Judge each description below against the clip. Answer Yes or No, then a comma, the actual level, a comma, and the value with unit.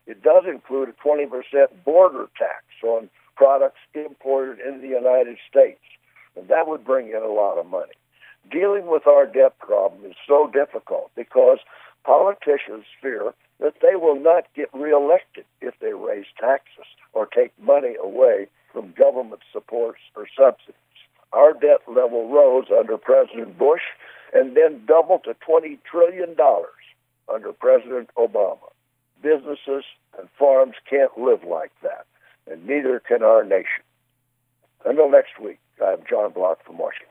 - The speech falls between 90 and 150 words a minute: Yes, average, 140 wpm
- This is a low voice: No, medium, 160 Hz